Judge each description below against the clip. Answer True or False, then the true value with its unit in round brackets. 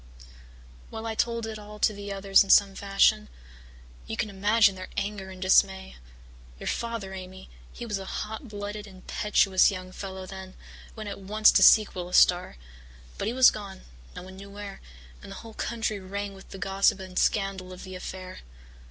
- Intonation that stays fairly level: True (1.9 semitones)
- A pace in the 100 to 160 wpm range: False (185 wpm)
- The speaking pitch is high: True (195 Hz)